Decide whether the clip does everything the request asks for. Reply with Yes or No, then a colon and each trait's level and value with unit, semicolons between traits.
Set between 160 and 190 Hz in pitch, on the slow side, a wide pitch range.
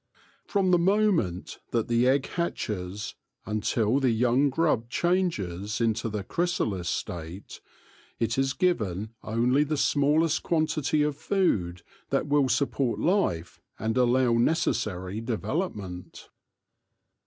No: low, 120 Hz; slow, 115 wpm; wide, 6.6 semitones